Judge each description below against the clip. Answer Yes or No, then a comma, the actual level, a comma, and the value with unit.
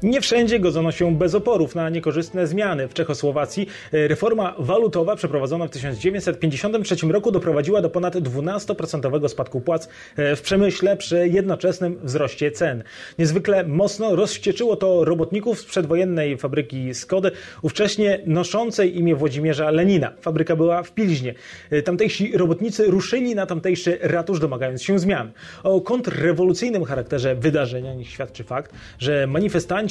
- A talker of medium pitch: Yes, medium, 170 Hz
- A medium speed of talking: Yes, average, 130 wpm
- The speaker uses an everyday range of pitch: Yes, average, 4.5 semitones